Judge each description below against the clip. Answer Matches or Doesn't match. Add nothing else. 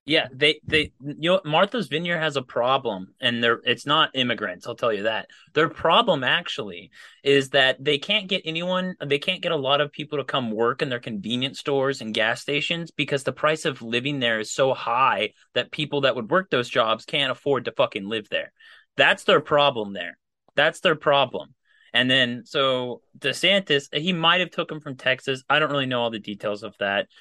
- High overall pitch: Doesn't match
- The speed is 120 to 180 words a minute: Doesn't match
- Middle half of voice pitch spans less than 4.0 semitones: Doesn't match